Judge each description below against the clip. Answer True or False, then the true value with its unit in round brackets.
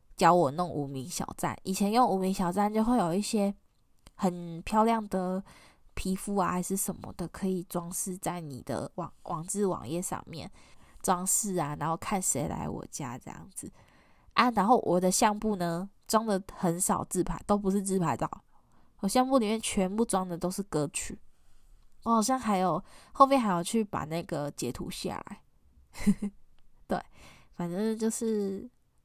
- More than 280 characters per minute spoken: False (235 characters per minute)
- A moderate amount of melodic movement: True (3.1 semitones)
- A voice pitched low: False (190 Hz)